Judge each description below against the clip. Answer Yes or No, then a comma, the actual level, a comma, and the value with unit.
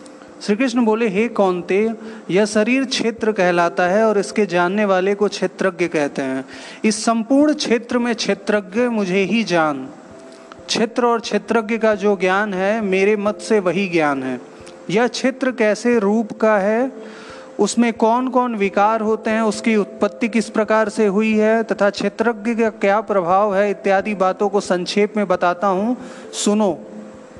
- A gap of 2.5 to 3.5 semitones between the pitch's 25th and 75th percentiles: Yes, average, 2.9 semitones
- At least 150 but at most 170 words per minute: Yes, average, 160 wpm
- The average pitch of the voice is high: Yes, high, 210 Hz